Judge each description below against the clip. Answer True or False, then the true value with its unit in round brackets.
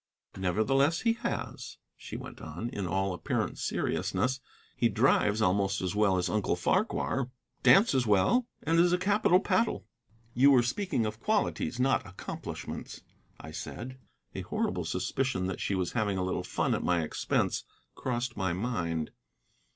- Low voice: True (110 Hz)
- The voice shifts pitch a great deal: True (6.4 semitones)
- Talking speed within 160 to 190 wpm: False (150 wpm)